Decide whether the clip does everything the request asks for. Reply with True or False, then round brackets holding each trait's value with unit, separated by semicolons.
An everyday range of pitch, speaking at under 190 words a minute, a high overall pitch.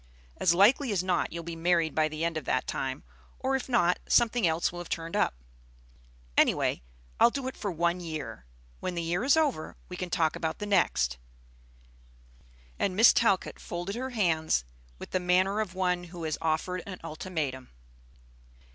False (3.7 semitones; 180 wpm; 175 Hz)